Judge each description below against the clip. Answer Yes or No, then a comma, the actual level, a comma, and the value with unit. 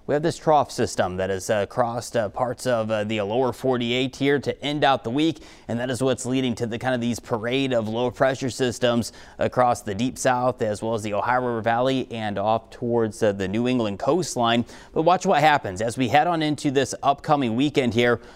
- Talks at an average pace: No, fast, 225 wpm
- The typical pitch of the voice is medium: No, low, 120 Hz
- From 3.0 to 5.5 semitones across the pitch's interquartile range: No, narrow, 2.4 semitones